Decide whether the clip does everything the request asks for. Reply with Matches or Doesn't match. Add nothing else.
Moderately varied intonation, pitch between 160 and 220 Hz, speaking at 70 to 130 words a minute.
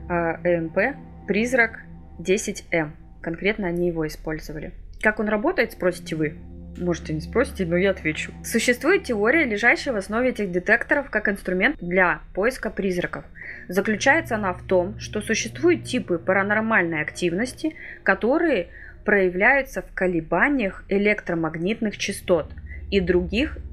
Matches